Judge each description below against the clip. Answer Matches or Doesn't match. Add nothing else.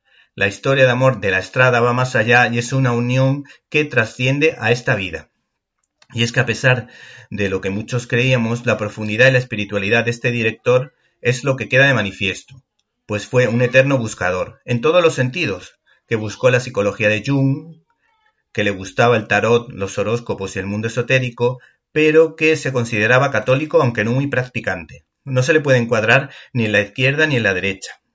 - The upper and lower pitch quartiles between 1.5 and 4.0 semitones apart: Matches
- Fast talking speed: Matches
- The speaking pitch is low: Matches